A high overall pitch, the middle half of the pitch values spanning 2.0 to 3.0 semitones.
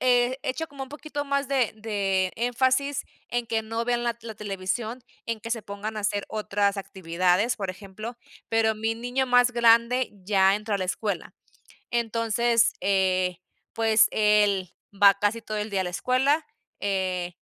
No: high, 220 Hz; average, 3.5 semitones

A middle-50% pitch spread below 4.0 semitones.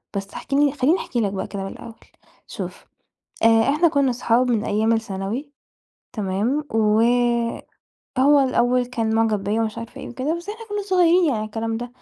No: average, 4.7 semitones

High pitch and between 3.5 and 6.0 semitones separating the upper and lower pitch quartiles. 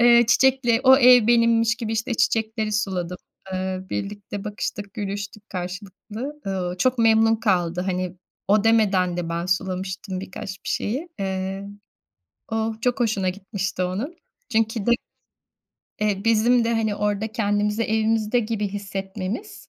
No: high, 210 Hz; average, 3.0 semitones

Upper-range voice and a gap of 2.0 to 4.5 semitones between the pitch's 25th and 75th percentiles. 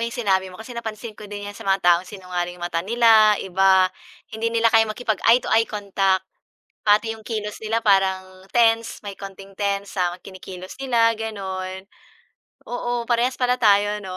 Yes: high, 205 Hz; average, 3.1 semitones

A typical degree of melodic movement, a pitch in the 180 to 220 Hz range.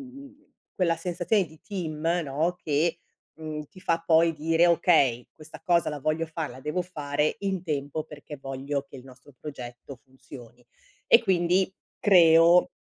No: average, 3.4 semitones; medium, 160 Hz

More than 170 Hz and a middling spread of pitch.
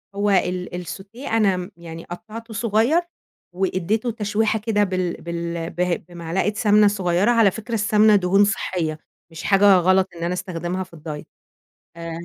Yes: high, 190 Hz; average, 3.4 semitones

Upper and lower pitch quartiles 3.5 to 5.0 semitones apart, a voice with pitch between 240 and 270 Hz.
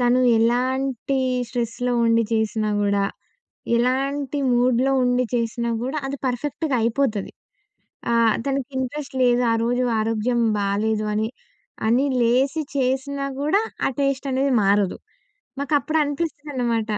No: average, 3.1 semitones; very high, 250 Hz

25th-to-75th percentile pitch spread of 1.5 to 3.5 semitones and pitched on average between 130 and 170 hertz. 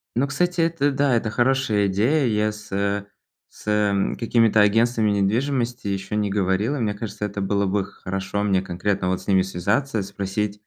No: average, 3.2 semitones; low, 105 Hz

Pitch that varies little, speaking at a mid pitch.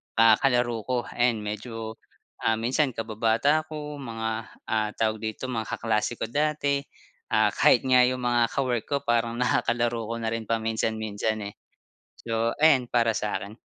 No: narrow, 2.2 semitones; low, 115 Hz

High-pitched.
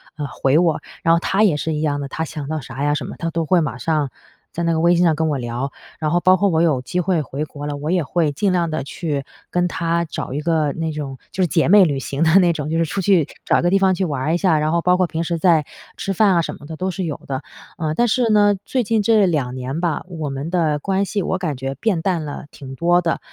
No: medium, 165 Hz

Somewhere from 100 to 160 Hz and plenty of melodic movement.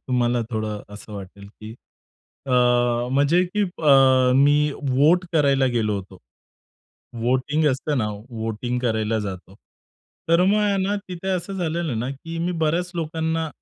Yes: medium, 140 Hz; wide, 6.9 semitones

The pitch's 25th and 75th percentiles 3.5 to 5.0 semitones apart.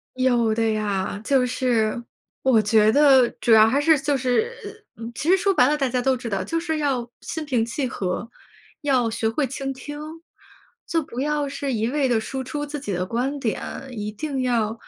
Yes: average, 4.2 semitones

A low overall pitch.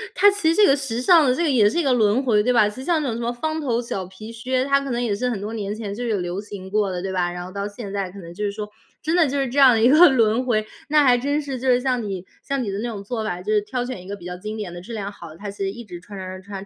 No: high, 220 Hz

